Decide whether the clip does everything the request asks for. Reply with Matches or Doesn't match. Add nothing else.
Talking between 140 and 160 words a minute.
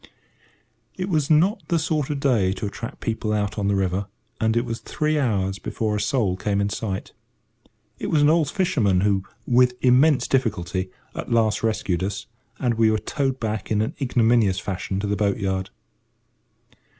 Doesn't match